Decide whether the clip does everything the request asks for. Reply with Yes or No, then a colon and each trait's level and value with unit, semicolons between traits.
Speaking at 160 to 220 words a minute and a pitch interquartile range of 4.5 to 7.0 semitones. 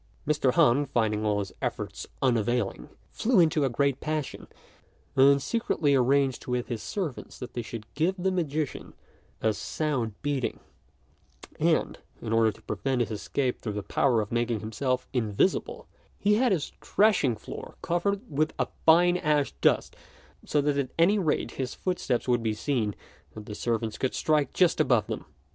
Yes: average, 165 wpm; average, 5.2 semitones